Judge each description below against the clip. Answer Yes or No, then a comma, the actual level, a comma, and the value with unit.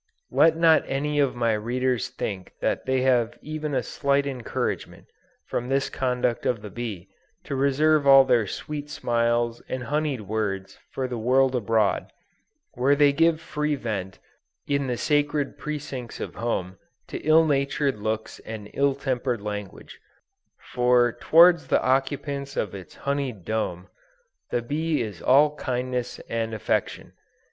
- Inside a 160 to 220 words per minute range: No, average, 145 wpm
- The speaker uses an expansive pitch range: No, average, 3.8 semitones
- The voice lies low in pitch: Yes, low, 130 Hz